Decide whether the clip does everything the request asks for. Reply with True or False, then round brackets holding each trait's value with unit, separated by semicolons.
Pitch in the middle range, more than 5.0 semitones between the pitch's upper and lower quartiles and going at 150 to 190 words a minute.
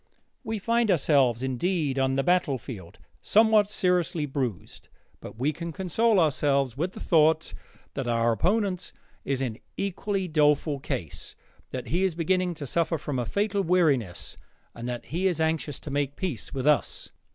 True (155 Hz; 5.5 semitones; 160 wpm)